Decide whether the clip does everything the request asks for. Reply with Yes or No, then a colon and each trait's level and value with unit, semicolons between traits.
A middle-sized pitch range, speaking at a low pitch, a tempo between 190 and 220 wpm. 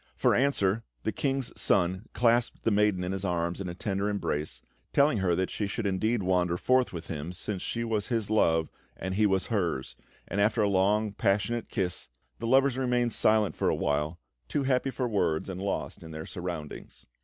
Yes: average, 4.3 semitones; low, 100 Hz; average, 195 wpm